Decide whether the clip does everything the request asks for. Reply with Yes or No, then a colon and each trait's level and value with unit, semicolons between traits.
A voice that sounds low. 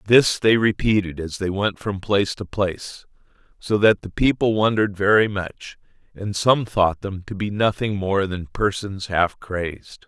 Yes: low, 100 Hz